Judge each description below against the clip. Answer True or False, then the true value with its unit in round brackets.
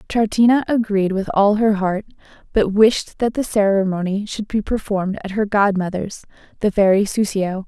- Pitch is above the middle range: True (205 Hz)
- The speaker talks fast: False (155 wpm)